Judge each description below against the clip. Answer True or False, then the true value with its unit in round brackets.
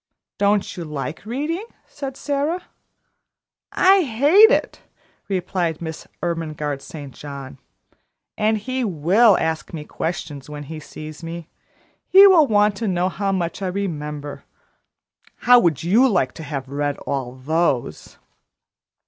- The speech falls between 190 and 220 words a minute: False (135 wpm)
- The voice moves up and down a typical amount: False (7.0 semitones)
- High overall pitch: False (175 Hz)